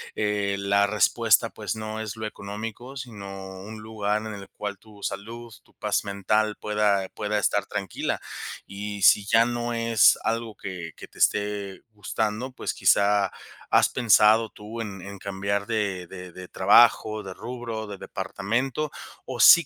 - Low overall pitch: Yes, low, 105 Hz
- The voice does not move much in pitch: Yes, narrow, 2.0 semitones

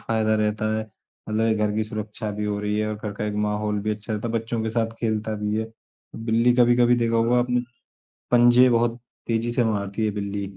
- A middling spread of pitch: No, narrow, 1.7 semitones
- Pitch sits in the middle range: No, low, 110 Hz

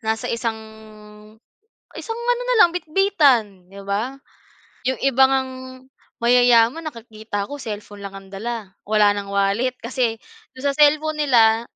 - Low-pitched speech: No, high, 235 Hz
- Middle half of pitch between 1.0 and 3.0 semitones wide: No, average, 4.9 semitones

